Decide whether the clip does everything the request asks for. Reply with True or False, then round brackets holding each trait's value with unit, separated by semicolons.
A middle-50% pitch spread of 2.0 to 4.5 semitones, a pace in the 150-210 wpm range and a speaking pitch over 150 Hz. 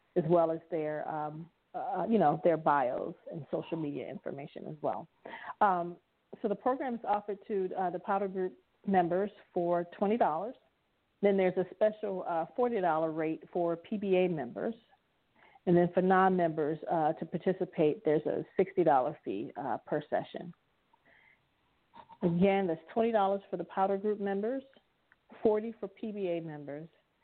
True (3.4 semitones; 155 wpm; 185 Hz)